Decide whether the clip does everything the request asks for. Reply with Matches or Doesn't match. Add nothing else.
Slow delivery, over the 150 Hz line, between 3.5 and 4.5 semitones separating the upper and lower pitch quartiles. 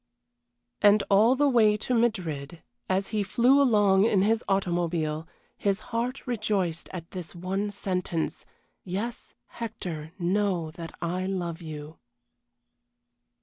Matches